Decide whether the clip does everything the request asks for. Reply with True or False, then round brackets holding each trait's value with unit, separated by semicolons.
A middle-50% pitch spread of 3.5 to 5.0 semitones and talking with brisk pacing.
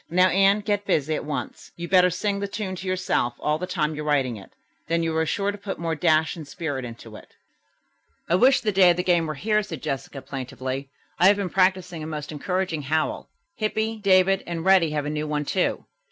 True (4.2 semitones; 225 wpm)